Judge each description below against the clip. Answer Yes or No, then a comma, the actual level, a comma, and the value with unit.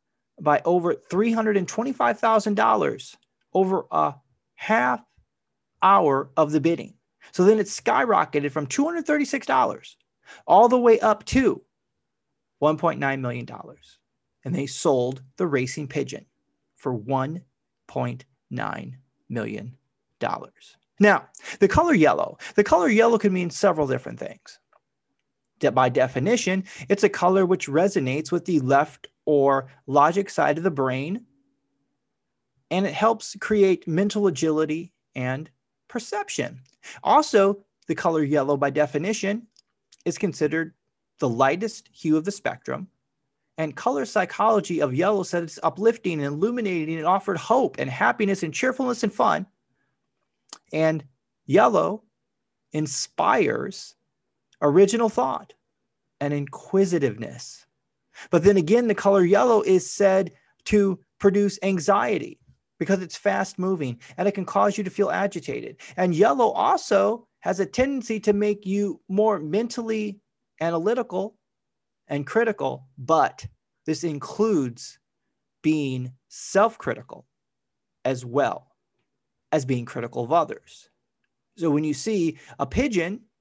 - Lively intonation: Yes, wide, 6.0 semitones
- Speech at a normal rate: No, slow, 120 wpm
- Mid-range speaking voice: Yes, medium, 180 Hz